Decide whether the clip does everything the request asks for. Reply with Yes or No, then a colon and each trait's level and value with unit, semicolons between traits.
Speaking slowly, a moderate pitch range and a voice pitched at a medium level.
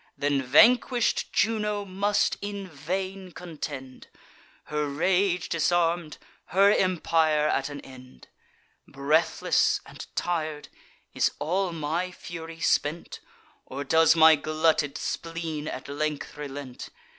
Yes: slow, 110 wpm; average, 3.8 semitones; medium, 160 Hz